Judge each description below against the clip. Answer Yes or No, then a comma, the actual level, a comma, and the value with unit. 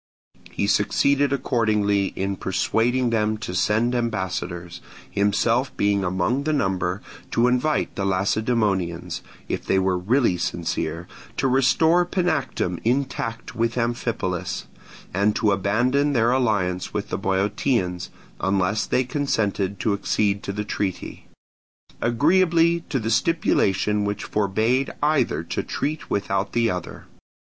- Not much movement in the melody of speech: No, average, 4.9 semitones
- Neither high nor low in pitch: No, low, 110 Hz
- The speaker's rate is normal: No, slow, 125 wpm